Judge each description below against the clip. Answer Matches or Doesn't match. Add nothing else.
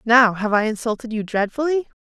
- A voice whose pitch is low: Doesn't match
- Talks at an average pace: Matches